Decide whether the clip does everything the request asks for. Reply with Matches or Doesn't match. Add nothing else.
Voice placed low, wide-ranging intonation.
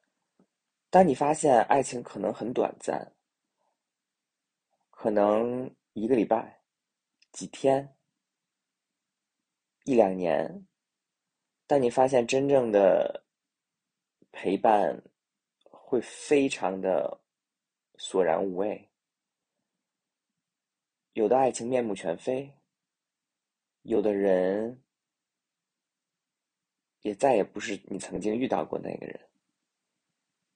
Doesn't match